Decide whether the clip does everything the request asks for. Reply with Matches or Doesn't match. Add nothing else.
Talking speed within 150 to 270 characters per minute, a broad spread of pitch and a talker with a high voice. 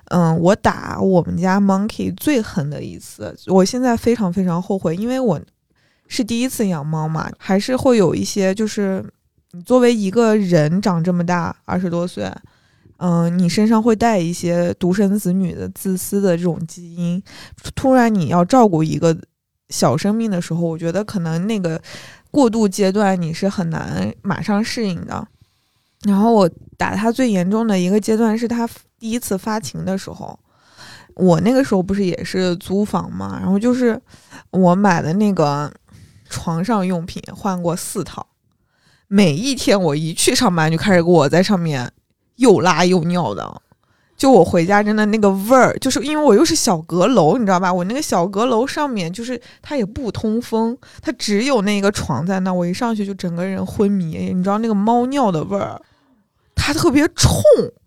Doesn't match